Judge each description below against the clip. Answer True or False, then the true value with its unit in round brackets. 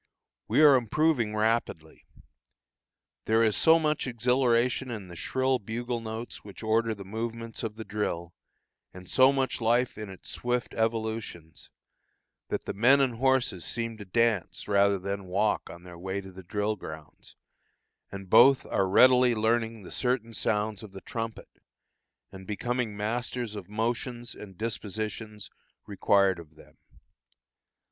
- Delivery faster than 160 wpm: False (145 wpm)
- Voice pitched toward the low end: True (110 Hz)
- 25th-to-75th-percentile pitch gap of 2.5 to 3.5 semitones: True (3.2 semitones)